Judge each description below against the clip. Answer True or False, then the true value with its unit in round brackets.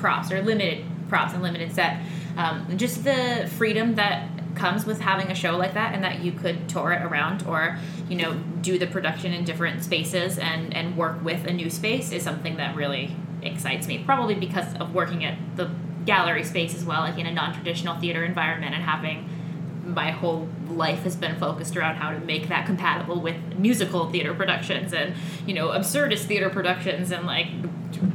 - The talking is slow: False (190 wpm)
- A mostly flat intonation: True (1.7 semitones)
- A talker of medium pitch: True (170 Hz)